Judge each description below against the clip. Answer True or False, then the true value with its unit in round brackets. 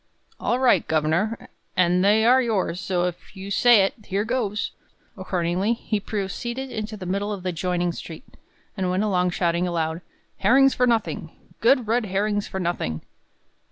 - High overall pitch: True (195 Hz)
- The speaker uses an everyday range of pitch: True (3.6 semitones)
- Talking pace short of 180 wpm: True (160 wpm)